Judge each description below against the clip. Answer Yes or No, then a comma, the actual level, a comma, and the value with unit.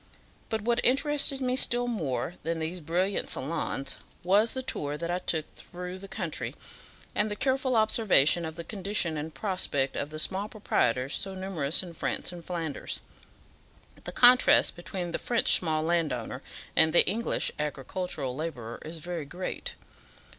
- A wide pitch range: No, average, 5.0 semitones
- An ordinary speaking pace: Yes, average, 155 wpm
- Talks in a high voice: No, medium, 175 Hz